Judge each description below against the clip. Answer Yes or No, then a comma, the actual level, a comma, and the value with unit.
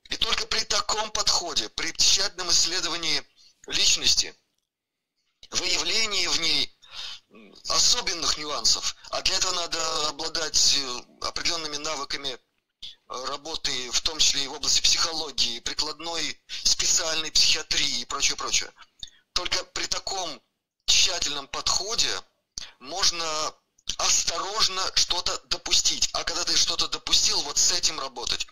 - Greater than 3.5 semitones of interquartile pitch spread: No, average, 3.2 semitones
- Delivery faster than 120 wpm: No, slow, 110 wpm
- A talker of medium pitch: Yes, medium, 160 Hz